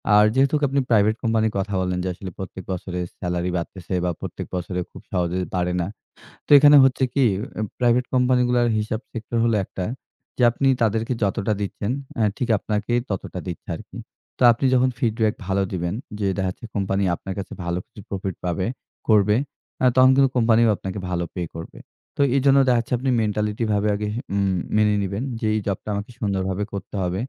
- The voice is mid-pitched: No, low, 105 Hz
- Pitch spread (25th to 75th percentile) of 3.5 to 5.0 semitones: Yes, average, 3.8 semitones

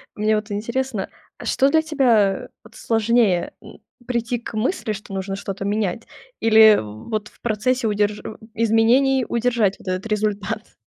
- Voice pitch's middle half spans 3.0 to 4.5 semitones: No, narrow, 2.5 semitones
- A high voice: Yes, high, 220 Hz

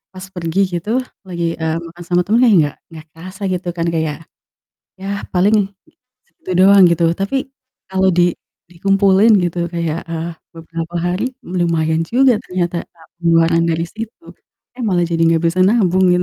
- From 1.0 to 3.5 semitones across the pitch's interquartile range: Yes, narrow, 2.6 semitones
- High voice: No, medium, 175 Hz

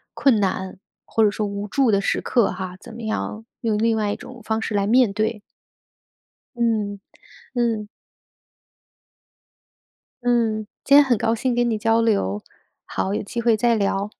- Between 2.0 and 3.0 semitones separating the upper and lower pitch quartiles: Yes, narrow, 2.5 semitones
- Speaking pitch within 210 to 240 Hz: Yes, high, 220 Hz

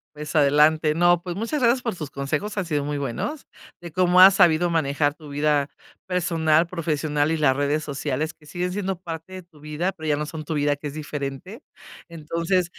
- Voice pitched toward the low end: No, medium, 160 Hz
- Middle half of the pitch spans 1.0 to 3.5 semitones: Yes, average, 3.2 semitones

